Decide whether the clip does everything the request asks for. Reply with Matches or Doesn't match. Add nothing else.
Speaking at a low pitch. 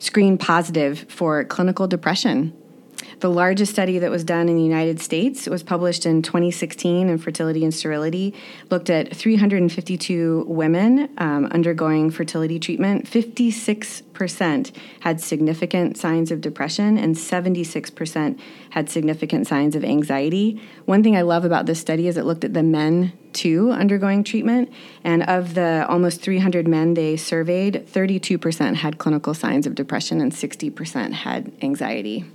Doesn't match